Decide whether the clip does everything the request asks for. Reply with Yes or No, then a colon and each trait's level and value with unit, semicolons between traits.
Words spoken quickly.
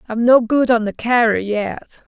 No: average, 195 wpm